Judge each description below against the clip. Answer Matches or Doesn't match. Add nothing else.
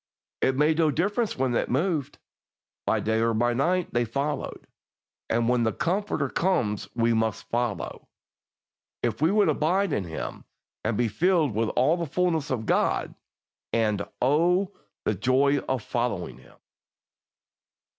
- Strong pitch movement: Matches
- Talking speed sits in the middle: Matches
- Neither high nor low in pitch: Doesn't match